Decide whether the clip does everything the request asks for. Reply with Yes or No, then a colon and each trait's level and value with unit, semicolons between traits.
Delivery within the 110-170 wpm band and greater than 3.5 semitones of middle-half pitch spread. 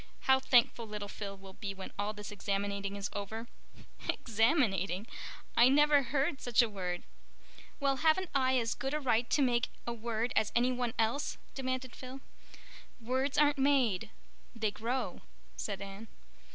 Yes: average, 150 wpm; average, 4.5 semitones